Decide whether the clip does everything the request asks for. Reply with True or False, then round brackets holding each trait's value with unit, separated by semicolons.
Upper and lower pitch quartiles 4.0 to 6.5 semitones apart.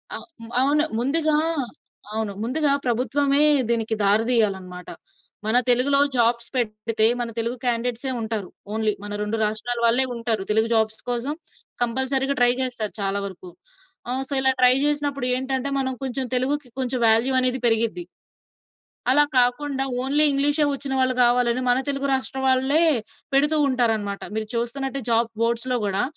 False (3.0 semitones)